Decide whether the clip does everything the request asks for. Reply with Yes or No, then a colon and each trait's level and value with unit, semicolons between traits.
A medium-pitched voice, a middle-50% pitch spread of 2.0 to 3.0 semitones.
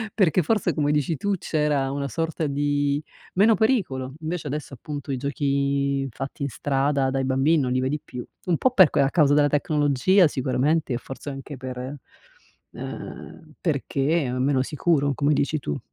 Yes: medium, 145 Hz; narrow, 2.5 semitones